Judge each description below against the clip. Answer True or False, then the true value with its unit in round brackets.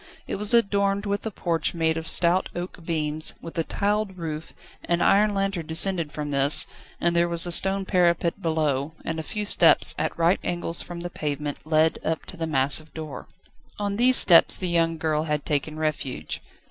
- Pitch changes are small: False (3.4 semitones)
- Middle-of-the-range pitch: True (165 Hz)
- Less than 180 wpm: False (190 wpm)